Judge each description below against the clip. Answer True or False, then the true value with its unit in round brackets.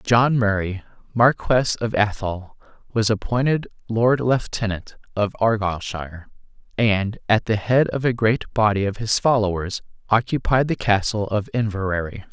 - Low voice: True (110 Hz)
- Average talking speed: False (130 wpm)